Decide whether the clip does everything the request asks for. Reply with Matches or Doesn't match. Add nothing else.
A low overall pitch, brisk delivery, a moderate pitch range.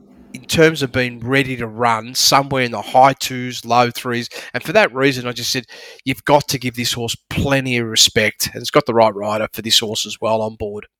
Matches